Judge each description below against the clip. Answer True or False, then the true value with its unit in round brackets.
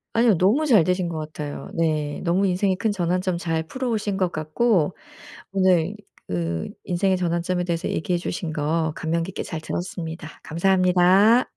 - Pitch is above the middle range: False (175 Hz)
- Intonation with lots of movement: False (3.0 semitones)